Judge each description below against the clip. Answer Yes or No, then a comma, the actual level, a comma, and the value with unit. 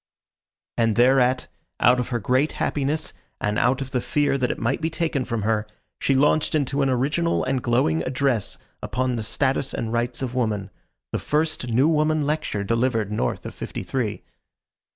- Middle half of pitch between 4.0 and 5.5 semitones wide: No, average, 3.3 semitones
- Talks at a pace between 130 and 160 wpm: No, average, 175 wpm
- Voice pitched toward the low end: Yes, low, 130 Hz